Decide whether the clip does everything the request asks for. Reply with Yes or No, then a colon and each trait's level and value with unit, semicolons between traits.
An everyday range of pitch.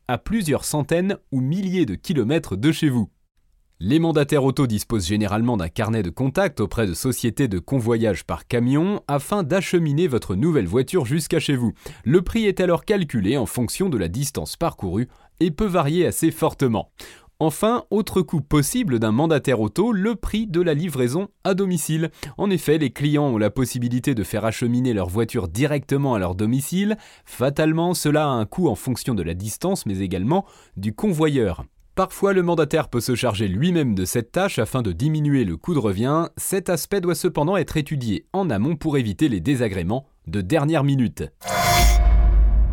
No: wide, 7.1 semitones